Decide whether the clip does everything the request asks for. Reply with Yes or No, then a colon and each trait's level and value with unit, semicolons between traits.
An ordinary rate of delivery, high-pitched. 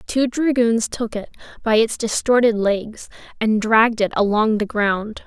Yes: average, 160 wpm; high, 220 Hz